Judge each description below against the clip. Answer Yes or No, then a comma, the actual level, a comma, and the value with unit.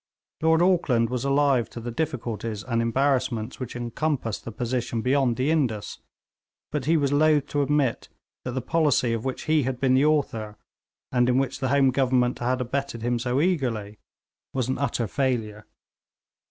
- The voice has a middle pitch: No, low, 130 Hz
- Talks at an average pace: Yes, average, 170 wpm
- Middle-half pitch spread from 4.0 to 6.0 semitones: No, average, 3.2 semitones